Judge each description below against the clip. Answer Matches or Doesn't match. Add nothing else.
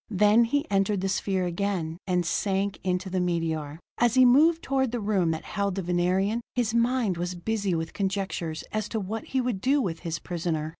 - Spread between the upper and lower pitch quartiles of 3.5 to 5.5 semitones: Matches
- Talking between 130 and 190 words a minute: Doesn't match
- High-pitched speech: Matches